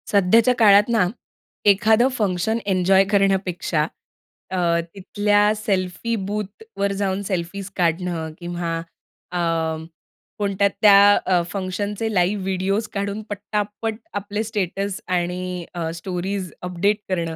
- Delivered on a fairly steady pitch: Yes, narrow, 2.3 semitones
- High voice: Yes, high, 195 Hz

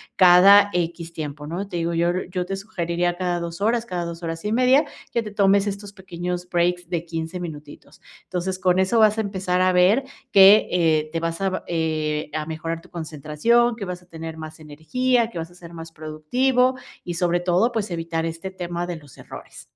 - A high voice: No, medium, 175 Hz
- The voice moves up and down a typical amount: Yes, average, 3.1 semitones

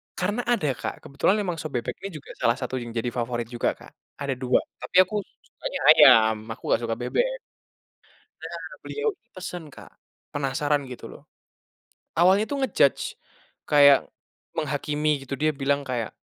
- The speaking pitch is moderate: Yes, medium, 145 Hz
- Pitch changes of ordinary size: No, wide, 6.7 semitones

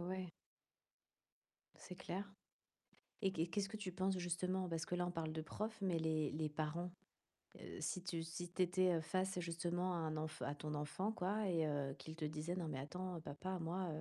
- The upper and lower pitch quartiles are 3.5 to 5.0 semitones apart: No, average, 2.8 semitones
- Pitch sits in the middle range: Yes, medium, 175 Hz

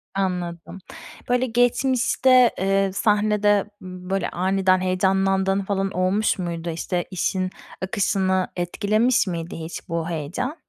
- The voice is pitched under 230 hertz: Yes, high, 190 Hz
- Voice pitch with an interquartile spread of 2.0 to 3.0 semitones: Yes, narrow, 2.4 semitones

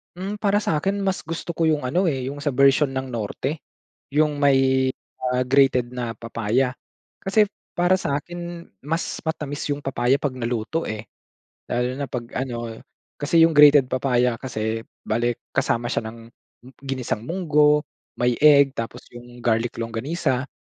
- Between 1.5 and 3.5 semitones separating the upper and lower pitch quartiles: No, average, 4.0 semitones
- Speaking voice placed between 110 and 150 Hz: Yes, low, 135 Hz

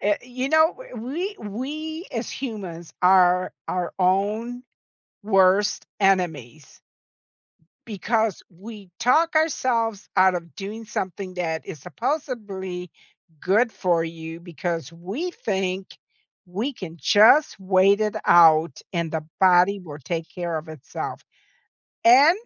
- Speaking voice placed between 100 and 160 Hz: No, high, 195 Hz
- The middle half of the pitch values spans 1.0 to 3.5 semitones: No, average, 4.8 semitones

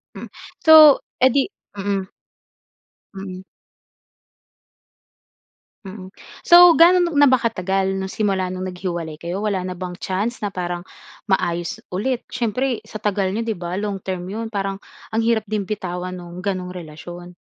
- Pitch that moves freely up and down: No, average, 3.3 semitones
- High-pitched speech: Yes, high, 195 Hz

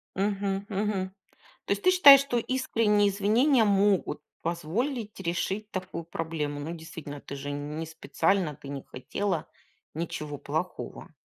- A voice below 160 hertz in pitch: No, high, 190 Hz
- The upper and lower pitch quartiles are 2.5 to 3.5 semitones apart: No, average, 4.8 semitones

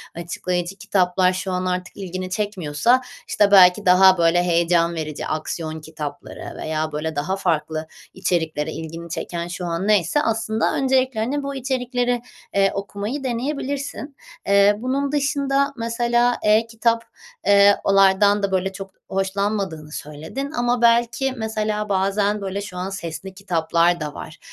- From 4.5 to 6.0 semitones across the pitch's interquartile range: Yes, average, 5.0 semitones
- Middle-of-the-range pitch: No, high, 195 Hz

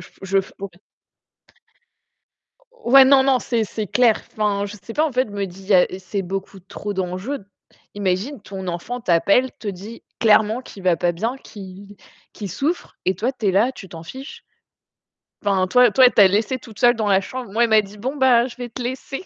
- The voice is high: Yes, high, 210 Hz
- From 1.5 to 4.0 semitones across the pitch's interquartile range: No, average, 4.5 semitones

